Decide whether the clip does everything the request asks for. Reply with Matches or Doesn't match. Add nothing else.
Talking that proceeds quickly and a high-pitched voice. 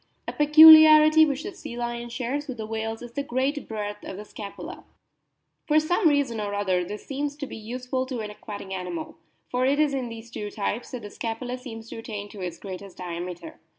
Matches